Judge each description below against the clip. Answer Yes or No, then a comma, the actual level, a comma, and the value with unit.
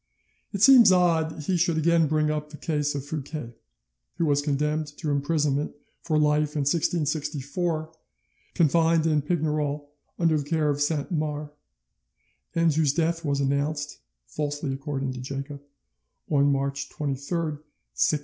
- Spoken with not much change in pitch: Yes, narrow, 2.1 semitones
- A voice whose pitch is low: No, medium, 150 Hz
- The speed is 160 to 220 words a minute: No, average, 145 wpm